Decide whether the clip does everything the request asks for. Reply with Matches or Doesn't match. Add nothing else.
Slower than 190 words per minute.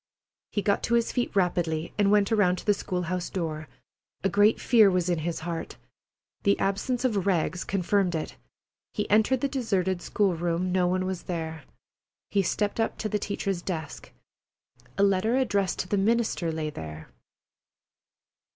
Matches